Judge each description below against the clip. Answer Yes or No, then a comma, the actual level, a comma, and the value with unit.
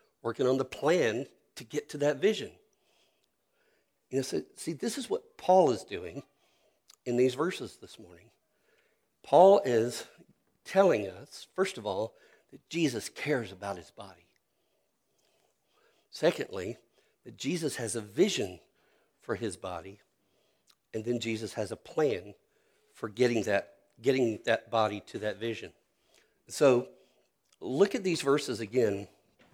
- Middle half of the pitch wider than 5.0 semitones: Yes, wide, 5.6 semitones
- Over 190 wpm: No, slow, 135 wpm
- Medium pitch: No, low, 120 Hz